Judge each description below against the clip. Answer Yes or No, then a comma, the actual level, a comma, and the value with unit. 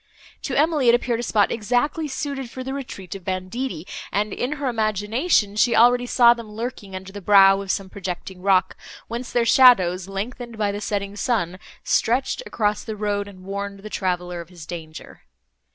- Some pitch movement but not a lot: Yes, average, 4.0 semitones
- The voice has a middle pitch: No, high, 210 Hz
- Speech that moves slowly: No, average, 185 wpm